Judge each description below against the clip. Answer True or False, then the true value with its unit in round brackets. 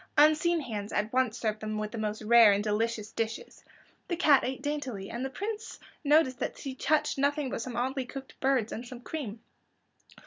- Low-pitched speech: False (250 Hz)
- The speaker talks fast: False (195 wpm)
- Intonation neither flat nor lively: True (4.8 semitones)